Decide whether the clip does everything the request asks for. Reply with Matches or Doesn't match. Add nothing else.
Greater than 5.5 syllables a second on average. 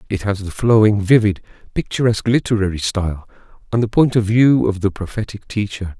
Matches